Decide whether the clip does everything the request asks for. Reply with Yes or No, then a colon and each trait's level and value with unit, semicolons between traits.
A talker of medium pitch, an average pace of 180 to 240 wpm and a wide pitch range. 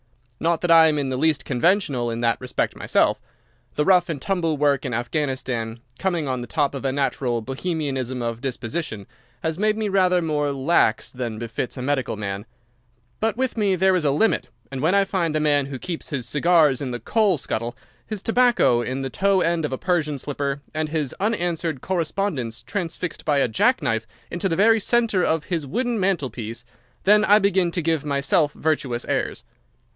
Yes: medium, 150 Hz; average, 190 wpm; wide, 5.7 semitones